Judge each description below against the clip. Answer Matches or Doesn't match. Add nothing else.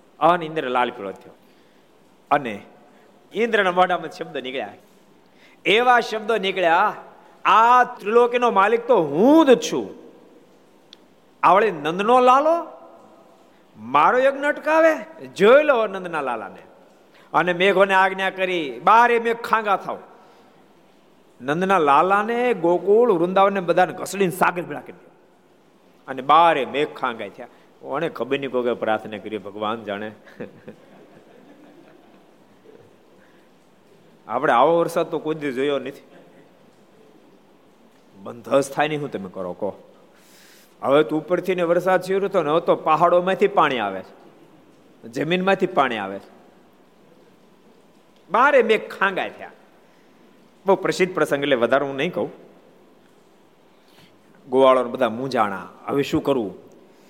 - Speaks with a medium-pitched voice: Matches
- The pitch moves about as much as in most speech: Doesn't match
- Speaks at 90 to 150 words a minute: Matches